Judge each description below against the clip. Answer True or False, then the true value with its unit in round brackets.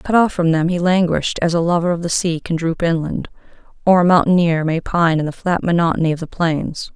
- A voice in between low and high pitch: True (170 Hz)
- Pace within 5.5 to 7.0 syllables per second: True (5.7 syllables/s)